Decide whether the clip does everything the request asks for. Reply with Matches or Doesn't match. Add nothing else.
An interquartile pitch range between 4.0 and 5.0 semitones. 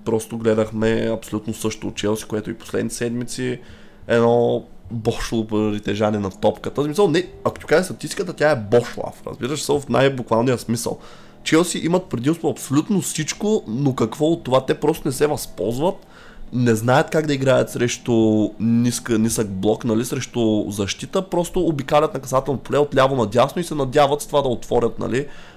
Matches